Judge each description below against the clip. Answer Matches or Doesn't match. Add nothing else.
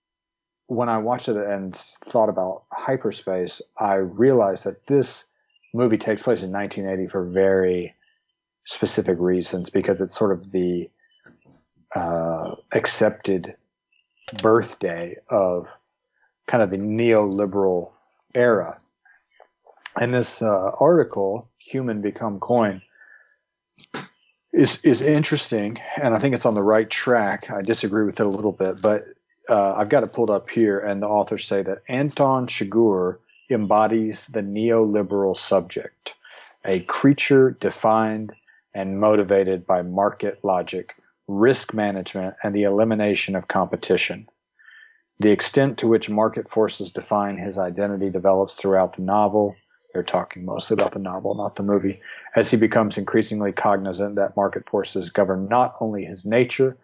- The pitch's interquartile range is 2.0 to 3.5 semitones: Matches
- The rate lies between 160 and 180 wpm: Doesn't match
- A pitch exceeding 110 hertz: Doesn't match